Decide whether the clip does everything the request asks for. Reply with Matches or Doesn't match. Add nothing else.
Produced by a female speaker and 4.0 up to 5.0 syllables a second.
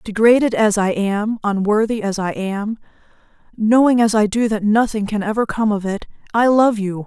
Matches